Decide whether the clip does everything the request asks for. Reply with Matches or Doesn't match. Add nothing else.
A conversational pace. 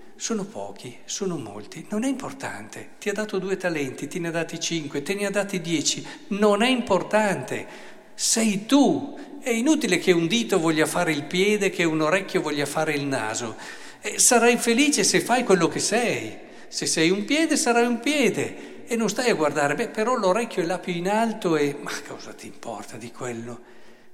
Doesn't match